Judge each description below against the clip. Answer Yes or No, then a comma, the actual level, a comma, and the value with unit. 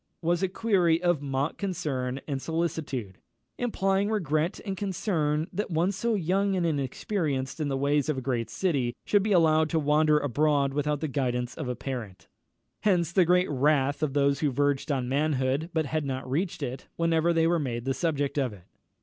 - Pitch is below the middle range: No, medium, 150 Hz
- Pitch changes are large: No, average, 4.1 semitones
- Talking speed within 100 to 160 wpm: No, average, 190 wpm